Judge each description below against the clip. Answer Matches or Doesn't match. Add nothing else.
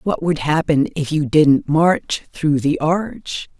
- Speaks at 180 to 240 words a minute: Doesn't match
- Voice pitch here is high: Doesn't match